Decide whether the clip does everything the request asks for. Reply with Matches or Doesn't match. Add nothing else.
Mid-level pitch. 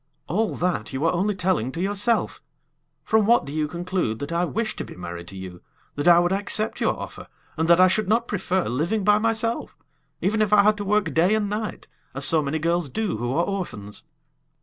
Matches